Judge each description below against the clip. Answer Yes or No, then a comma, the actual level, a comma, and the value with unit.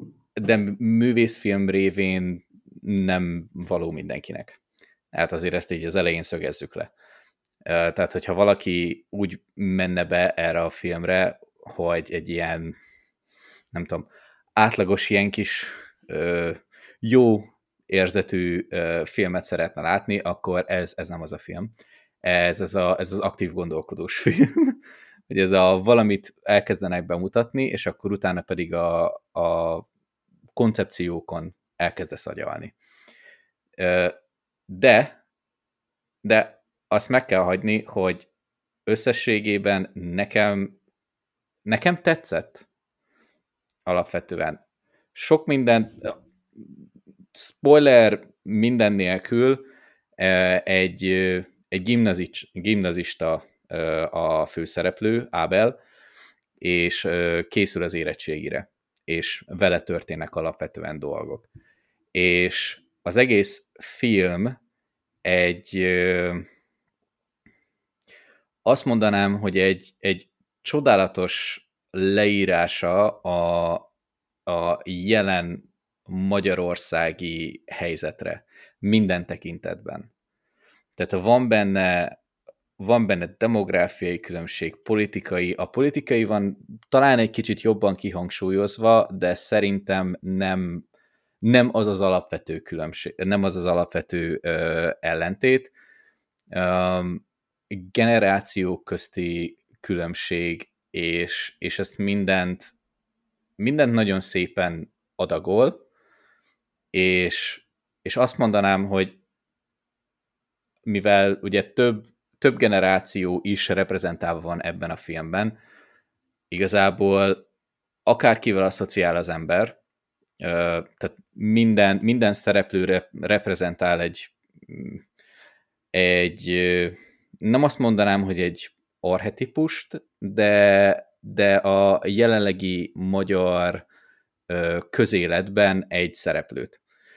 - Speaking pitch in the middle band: No, very low, 95 Hz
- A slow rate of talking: Yes, slow, 90 wpm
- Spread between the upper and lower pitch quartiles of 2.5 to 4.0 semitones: Yes, average, 2.8 semitones